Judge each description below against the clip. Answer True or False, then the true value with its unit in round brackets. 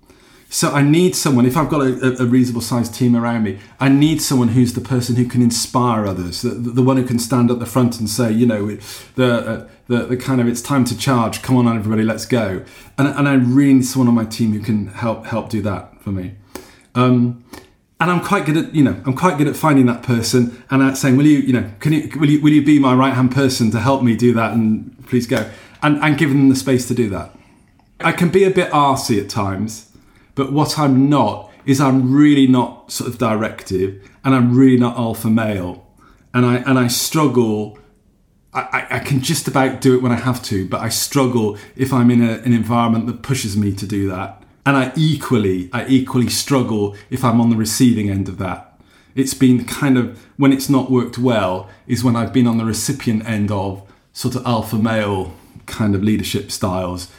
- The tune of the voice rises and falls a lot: False (3.4 semitones)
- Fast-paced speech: True (225 wpm)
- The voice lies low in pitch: True (120 Hz)